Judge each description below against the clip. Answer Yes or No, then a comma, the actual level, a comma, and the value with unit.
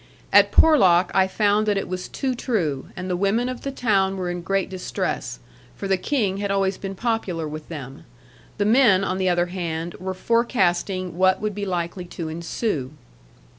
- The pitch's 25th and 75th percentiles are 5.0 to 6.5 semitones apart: No, average, 2.9 semitones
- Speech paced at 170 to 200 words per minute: Yes, average, 185 wpm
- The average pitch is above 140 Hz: Yes, high, 190 Hz